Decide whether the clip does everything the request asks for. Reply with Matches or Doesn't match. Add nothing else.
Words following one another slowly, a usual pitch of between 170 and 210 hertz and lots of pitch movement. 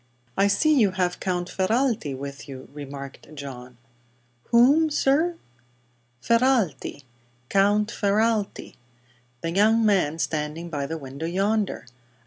Matches